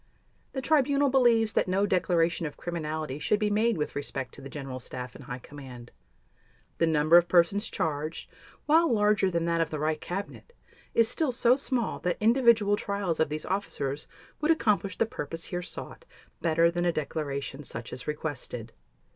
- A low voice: No, medium, 170 Hz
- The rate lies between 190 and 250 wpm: No, average, 175 wpm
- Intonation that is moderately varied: No, wide, 6.1 semitones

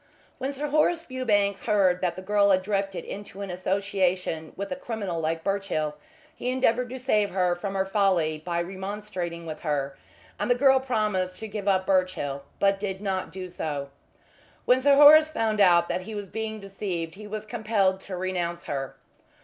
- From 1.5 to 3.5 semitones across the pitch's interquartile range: Yes, average, 3.1 semitones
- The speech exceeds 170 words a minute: Yes, average, 180 wpm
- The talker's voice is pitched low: No, high, 195 Hz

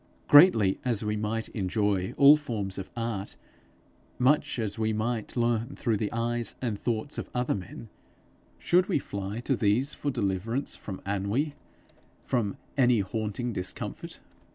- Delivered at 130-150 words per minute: Yes, average, 145 wpm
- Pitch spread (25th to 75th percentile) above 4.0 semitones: No, average, 3.4 semitones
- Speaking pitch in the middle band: No, low, 115 Hz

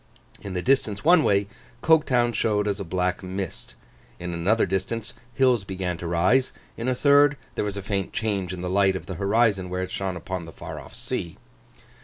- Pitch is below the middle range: Yes, low, 100 Hz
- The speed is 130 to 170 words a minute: No, average, 200 wpm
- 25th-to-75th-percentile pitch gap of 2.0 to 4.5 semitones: Yes, average, 4.0 semitones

